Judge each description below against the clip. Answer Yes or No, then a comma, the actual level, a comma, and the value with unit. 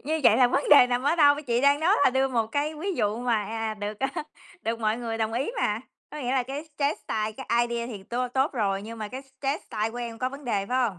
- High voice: Yes, high, 245 Hz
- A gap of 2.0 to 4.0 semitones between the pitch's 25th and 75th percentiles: Yes, average, 3.5 semitones